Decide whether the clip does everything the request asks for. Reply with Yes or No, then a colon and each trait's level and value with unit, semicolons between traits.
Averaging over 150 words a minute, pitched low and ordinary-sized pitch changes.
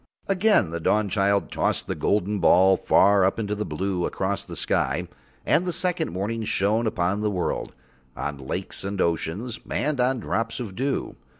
Yes: average, 170 wpm; low, 100 Hz; average, 3.9 semitones